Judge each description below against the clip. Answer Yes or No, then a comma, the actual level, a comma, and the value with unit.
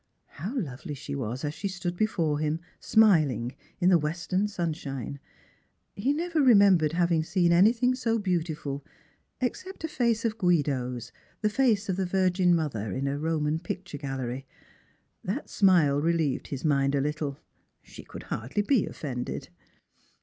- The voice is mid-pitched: Yes, medium, 170 Hz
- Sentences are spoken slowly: No, average, 160 wpm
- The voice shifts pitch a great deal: Yes, wide, 5.9 semitones